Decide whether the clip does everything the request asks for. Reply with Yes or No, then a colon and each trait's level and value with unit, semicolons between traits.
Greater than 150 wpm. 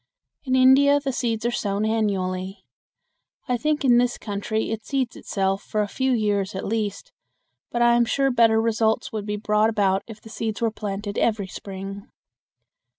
Yes: average, 175 wpm